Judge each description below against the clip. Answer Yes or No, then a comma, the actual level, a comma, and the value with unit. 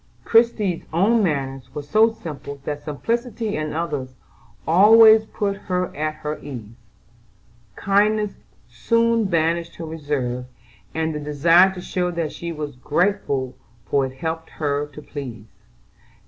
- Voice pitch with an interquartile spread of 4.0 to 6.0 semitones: Yes, wide, 5.6 semitones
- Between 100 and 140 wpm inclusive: Yes, slow, 135 wpm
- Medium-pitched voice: Yes, medium, 160 Hz